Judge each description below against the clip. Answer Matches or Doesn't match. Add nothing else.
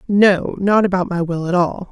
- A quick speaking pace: Matches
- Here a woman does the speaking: Matches